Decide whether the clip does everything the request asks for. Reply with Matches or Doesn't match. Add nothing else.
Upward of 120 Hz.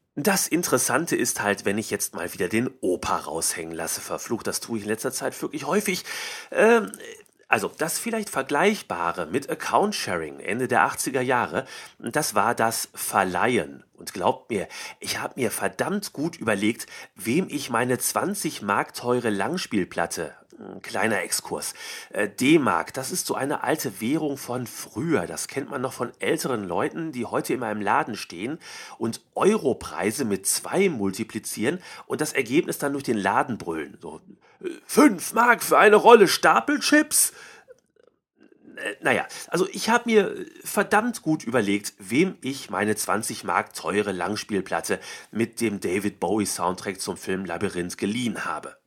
Matches